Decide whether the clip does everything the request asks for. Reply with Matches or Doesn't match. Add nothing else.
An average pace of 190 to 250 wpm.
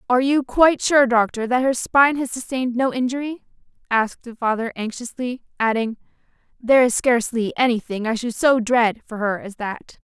Doesn't match